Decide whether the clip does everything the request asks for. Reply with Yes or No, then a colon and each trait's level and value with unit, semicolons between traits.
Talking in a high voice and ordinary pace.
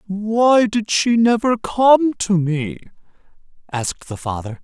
No: high, 200 Hz; slow, 130 wpm